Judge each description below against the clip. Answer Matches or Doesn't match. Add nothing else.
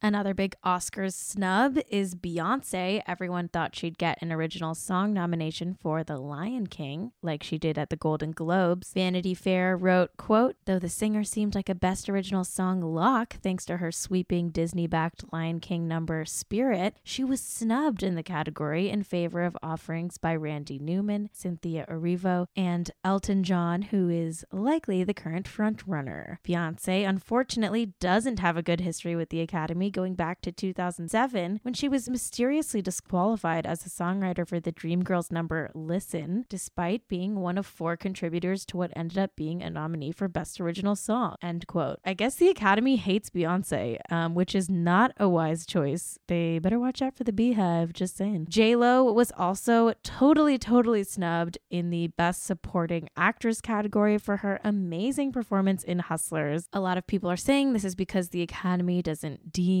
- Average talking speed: Matches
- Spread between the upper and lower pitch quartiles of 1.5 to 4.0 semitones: Matches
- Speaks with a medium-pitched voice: Matches